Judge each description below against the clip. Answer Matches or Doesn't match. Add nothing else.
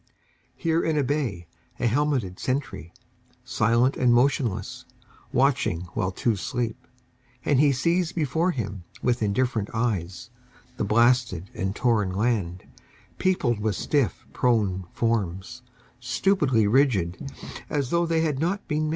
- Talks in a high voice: Doesn't match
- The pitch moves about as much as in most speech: Doesn't match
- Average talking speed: Doesn't match